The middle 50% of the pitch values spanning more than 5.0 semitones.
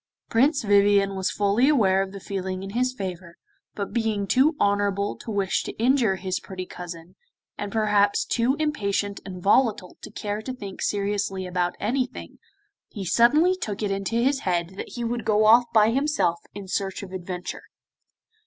No: average, 3.4 semitones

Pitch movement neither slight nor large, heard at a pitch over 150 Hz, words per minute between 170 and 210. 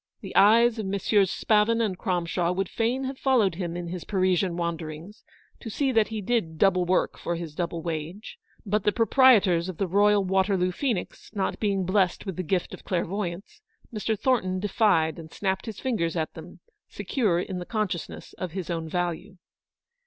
Yes: average, 3.5 semitones; high, 190 Hz; average, 180 wpm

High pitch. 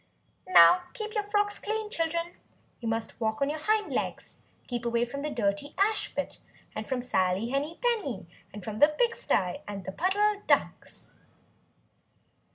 Yes: very high, 290 Hz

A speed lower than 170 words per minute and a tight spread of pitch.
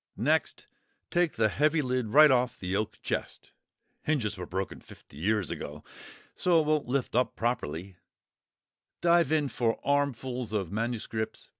No: average, 145 wpm; wide, 5.5 semitones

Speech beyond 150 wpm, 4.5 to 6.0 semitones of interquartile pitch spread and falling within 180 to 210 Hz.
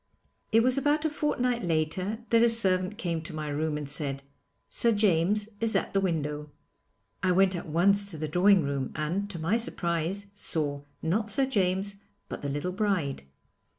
Yes: average, 180 wpm; average, 5.0 semitones; medium, 185 Hz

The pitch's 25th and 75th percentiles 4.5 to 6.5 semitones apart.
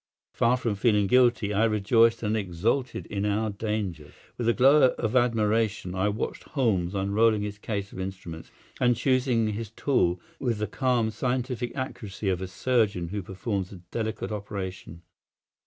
No: average, 3.2 semitones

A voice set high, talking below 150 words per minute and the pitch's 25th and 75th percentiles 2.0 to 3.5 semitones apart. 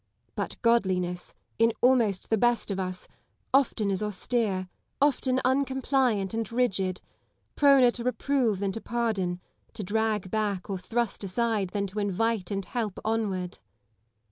No: high, 215 Hz; average, 140 wpm; average, 3.9 semitones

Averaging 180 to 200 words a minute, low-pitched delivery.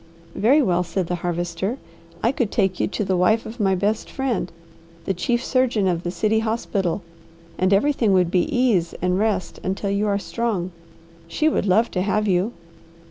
No: average, 185 wpm; high, 200 Hz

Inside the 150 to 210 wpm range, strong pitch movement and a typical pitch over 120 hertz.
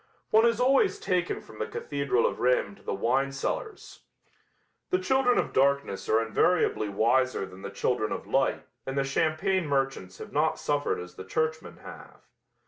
Yes: average, 170 wpm; wide, 8.0 semitones; medium, 140 Hz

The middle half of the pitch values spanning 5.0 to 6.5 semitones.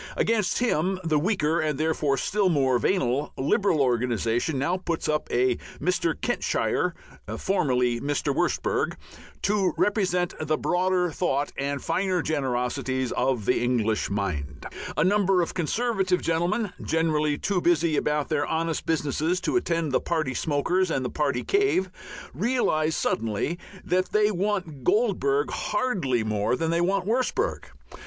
Yes: wide, 5.5 semitones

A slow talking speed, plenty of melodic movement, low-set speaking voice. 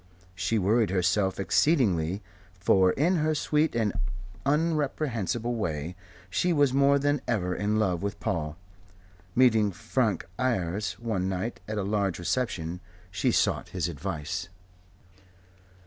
Yes: slow, 125 wpm; wide, 5.8 semitones; low, 105 Hz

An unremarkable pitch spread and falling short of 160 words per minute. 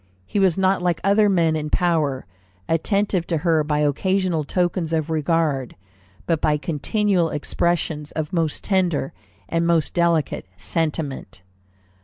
Yes: average, 3.0 semitones; slow, 135 wpm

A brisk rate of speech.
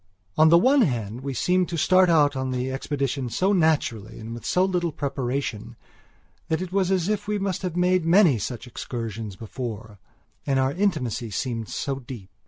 No: average, 185 wpm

